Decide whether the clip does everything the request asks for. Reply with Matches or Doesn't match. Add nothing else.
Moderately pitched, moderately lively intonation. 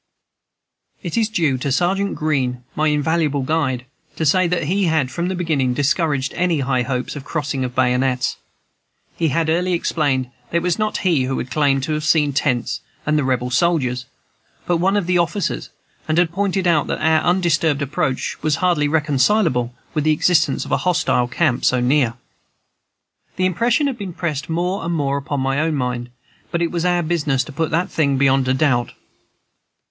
Matches